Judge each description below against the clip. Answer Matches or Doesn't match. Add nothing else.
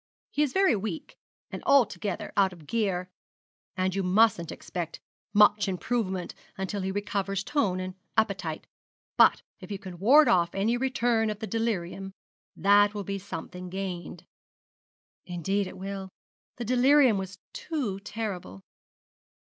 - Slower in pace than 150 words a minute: Matches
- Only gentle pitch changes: Doesn't match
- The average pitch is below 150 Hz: Doesn't match